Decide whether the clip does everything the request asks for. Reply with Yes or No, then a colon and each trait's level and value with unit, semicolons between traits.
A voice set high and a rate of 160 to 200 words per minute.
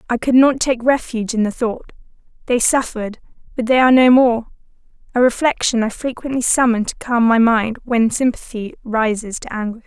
Yes: high, 235 Hz; average, 175 wpm